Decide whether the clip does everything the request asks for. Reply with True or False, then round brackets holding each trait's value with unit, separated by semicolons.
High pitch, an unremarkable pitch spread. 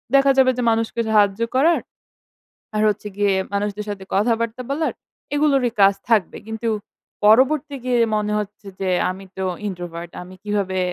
True (210 Hz; 4.0 semitones)